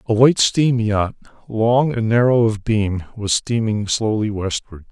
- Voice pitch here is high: No, low, 110 Hz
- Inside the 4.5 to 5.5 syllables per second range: No, 4.2 syllables/s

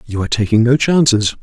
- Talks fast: Yes, fast, 210 wpm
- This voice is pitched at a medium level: No, low, 120 Hz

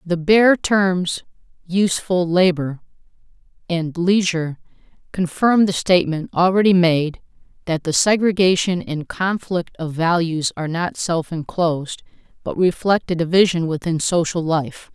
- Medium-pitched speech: Yes, medium, 175 Hz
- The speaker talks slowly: Yes, slow, 120 wpm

